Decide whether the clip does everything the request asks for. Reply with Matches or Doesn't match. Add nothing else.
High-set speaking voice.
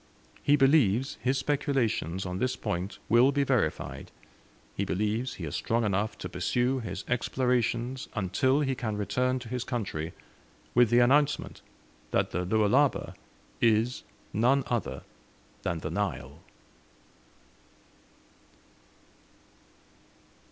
Doesn't match